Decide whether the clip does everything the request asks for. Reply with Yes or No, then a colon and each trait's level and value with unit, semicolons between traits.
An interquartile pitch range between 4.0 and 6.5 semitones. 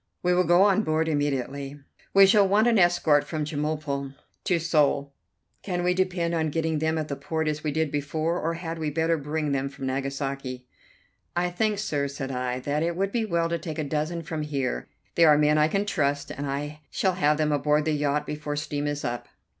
No: average, 2.8 semitones